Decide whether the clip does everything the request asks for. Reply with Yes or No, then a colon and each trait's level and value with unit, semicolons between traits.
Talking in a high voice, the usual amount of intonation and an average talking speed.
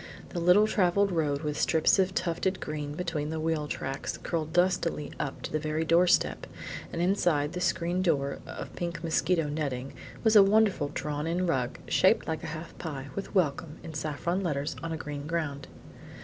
No: medium, 160 Hz; average, 3.1 semitones; average, 180 wpm